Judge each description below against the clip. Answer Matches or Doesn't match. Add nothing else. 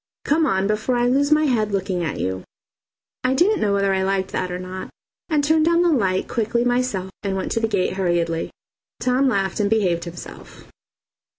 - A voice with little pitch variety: Doesn't match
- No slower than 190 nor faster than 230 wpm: Matches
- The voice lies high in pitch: Matches